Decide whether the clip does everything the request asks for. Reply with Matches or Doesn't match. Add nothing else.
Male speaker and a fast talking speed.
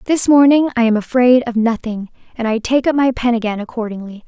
Doesn't match